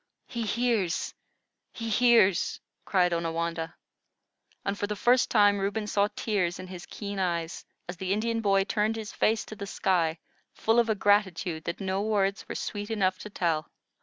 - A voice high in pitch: Yes, high, 200 Hz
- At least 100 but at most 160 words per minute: No, average, 170 wpm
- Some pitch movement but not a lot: Yes, average, 3.4 semitones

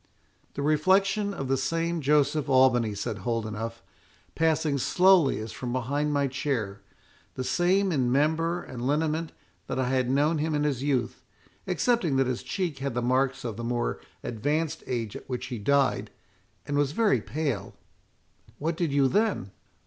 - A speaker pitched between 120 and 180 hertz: Yes, medium, 140 Hz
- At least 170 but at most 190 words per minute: No, average, 160 wpm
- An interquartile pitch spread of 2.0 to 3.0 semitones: No, average, 4.3 semitones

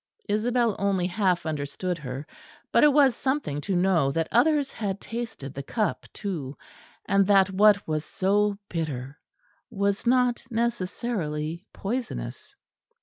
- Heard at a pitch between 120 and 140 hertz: No, high, 195 Hz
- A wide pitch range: Yes, wide, 6.3 semitones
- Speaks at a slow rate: Yes, slow, 130 wpm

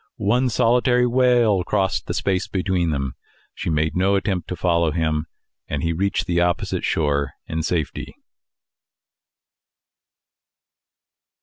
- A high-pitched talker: No, very low, 90 Hz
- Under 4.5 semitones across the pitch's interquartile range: Yes, average, 4.1 semitones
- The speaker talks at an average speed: No, slow, 115 wpm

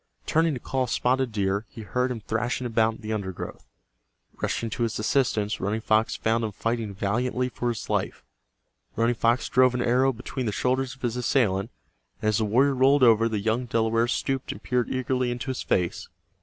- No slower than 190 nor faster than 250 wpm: Yes, average, 195 wpm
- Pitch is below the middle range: Yes, low, 120 Hz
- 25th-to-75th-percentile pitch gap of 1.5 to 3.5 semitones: Yes, narrow, 2.6 semitones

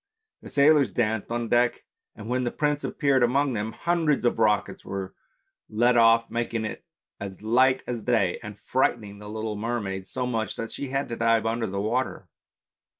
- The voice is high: No, low, 115 Hz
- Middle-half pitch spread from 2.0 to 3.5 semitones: Yes, average, 2.9 semitones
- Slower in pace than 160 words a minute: No, average, 180 wpm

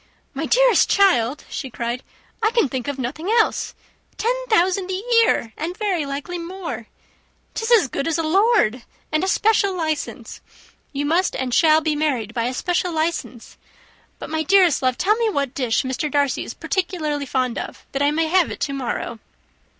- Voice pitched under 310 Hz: No, very high, 315 Hz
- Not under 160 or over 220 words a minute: Yes, average, 180 wpm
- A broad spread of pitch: Yes, wide, 5.8 semitones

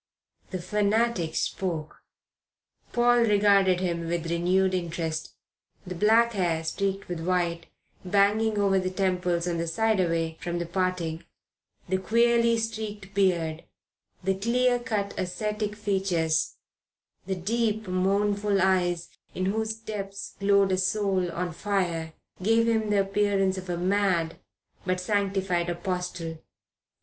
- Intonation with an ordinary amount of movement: Yes, average, 3.0 semitones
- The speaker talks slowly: Yes, slow, 125 wpm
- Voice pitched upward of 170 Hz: Yes, high, 190 Hz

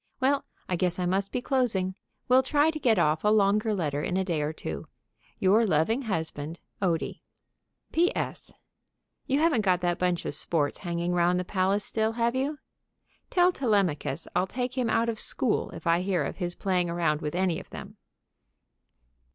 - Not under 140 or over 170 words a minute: No, average, 180 wpm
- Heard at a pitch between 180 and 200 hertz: Yes, high, 190 Hz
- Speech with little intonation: No, average, 5.3 semitones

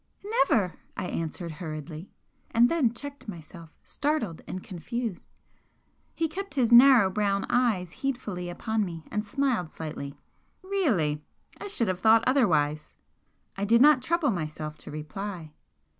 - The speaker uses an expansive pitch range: Yes, wide, 7.5 semitones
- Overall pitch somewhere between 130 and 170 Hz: No, high, 205 Hz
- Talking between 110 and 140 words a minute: Yes, slow, 135 wpm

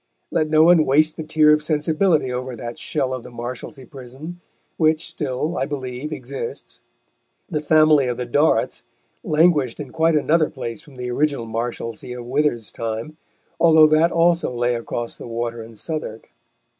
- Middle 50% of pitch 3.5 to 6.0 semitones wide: Yes, average, 4.3 semitones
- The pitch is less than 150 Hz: Yes, medium, 140 Hz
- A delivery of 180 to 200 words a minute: No, average, 165 wpm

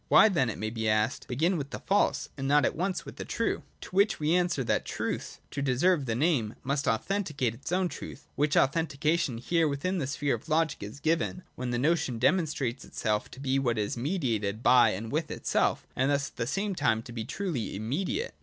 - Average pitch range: No, wide, 5.8 semitones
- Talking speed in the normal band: No, fast, 215 wpm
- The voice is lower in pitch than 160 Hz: Yes, medium, 140 Hz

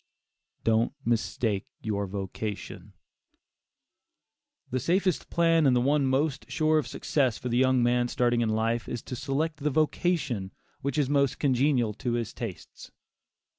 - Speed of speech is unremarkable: Yes, average, 145 wpm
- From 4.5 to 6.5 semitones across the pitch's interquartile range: No, average, 4.0 semitones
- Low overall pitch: Yes, low, 125 Hz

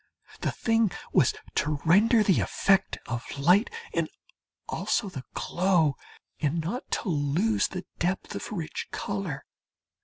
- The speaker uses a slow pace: Yes, slow, 130 wpm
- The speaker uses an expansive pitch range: No, average, 4.8 semitones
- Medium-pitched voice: Yes, medium, 180 Hz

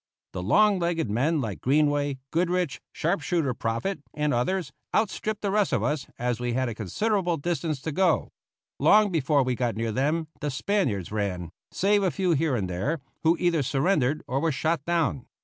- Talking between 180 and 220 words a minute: Yes, average, 185 wpm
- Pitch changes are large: Yes, wide, 6.1 semitones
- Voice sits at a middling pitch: Yes, medium, 150 Hz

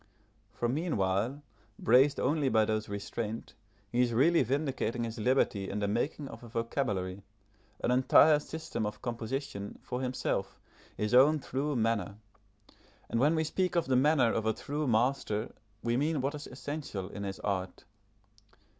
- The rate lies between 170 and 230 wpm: No, average, 155 wpm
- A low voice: Yes, low, 125 Hz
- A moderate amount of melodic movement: Yes, average, 4.7 semitones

